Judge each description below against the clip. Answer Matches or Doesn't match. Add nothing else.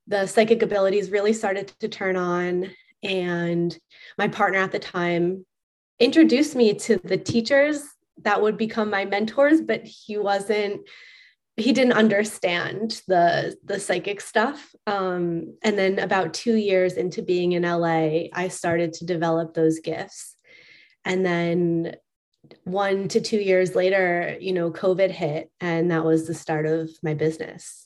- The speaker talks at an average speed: Matches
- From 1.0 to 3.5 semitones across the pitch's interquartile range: Doesn't match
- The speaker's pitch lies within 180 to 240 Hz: Matches